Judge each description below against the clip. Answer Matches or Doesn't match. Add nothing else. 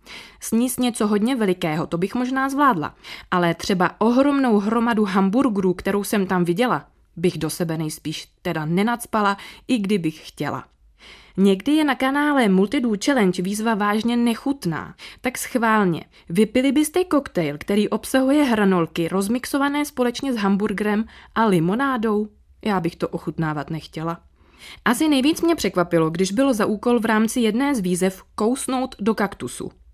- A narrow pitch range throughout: Doesn't match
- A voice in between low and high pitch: Doesn't match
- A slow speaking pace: Doesn't match